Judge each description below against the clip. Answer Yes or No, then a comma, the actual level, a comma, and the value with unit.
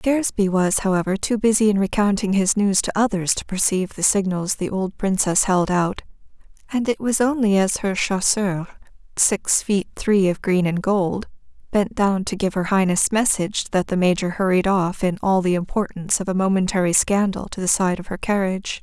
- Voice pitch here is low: No, high, 195 Hz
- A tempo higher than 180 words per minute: Yes, average, 190 wpm